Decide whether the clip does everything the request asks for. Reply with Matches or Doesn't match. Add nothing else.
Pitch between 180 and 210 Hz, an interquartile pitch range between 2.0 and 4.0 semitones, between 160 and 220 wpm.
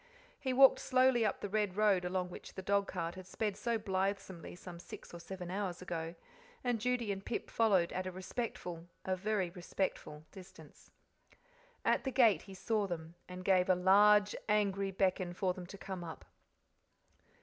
Matches